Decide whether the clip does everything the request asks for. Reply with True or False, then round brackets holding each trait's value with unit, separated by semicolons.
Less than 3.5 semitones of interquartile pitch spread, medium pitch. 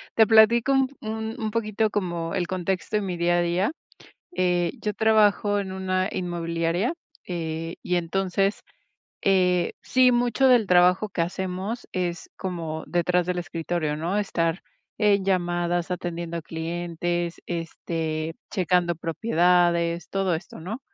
True (2.9 semitones; 180 Hz)